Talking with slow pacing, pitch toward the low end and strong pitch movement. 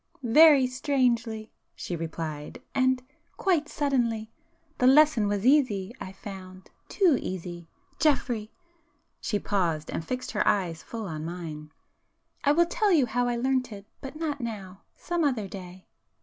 No: slow, 125 wpm; high, 230 Hz; wide, 6.9 semitones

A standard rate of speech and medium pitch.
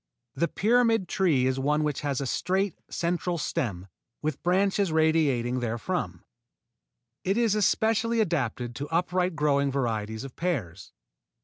No: slow, 130 wpm; medium, 155 Hz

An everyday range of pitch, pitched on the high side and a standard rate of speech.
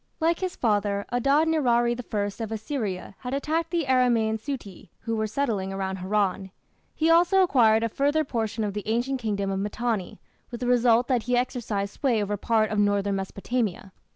Yes: average, 4.1 semitones; high, 230 Hz; average, 180 wpm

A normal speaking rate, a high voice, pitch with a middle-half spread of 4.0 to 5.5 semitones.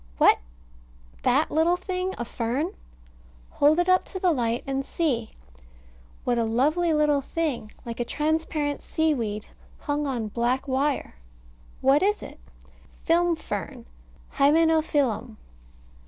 No: slow, 125 wpm; very high, 290 Hz; average, 5.1 semitones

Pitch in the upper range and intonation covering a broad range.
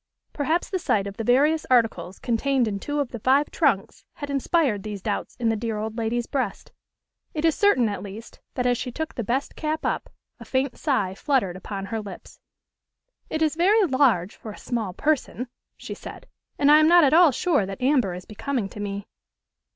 Yes: high, 245 Hz; wide, 5.8 semitones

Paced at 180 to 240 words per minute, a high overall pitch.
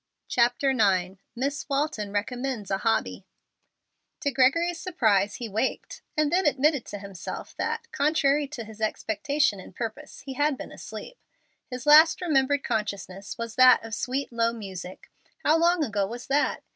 No: average, 160 wpm; very high, 255 Hz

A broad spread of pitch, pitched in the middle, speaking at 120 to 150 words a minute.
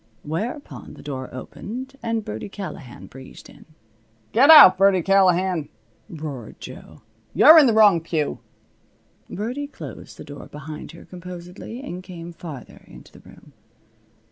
Yes: wide, 6.3 semitones; medium, 180 Hz; average, 140 wpm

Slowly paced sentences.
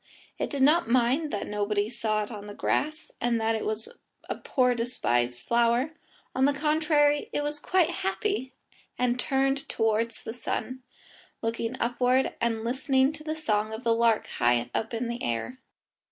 No: average, 170 wpm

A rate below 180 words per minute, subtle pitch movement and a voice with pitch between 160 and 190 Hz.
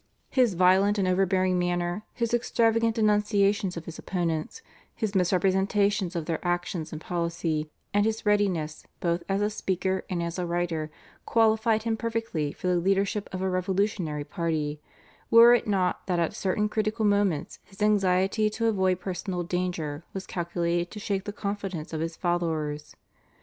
No: average, 160 wpm; average, 3.3 semitones; medium, 185 Hz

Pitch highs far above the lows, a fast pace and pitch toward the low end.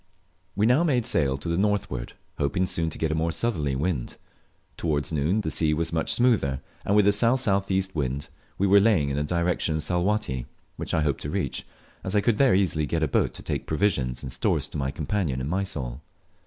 Yes: wide, 5.8 semitones; fast, 210 wpm; very low, 85 Hz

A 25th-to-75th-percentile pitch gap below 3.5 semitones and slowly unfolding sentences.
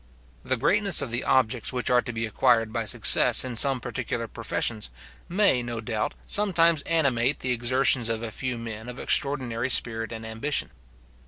No: average, 3.0 semitones; average, 170 wpm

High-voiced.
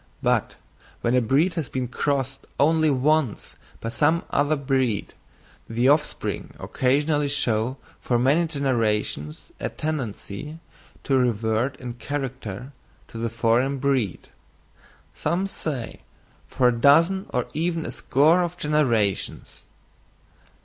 No: low, 135 Hz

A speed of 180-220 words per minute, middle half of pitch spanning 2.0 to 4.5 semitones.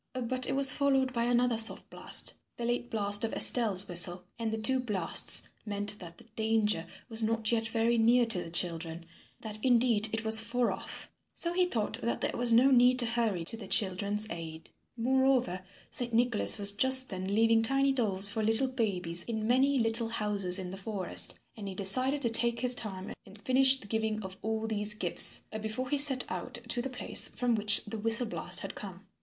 Yes: average, 200 wpm; average, 3.3 semitones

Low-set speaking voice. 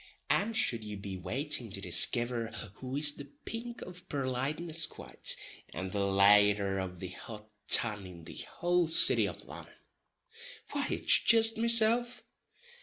Yes: low, 130 Hz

